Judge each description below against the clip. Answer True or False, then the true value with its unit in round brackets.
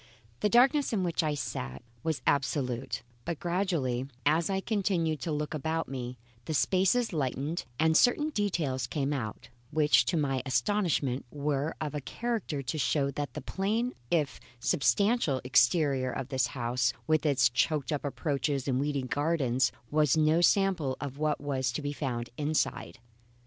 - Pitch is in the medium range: True (150 Hz)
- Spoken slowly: False (160 wpm)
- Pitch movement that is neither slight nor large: True (4.1 semitones)